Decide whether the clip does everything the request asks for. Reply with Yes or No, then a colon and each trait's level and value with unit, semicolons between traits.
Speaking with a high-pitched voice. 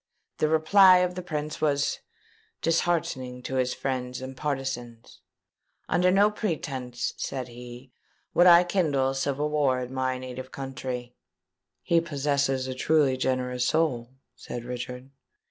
No: low, 135 Hz